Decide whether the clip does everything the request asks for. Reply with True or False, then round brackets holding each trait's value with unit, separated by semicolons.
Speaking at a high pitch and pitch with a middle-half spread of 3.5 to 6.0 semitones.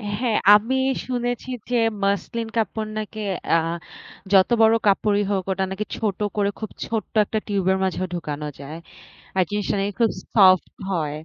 False (205 Hz; 2.8 semitones)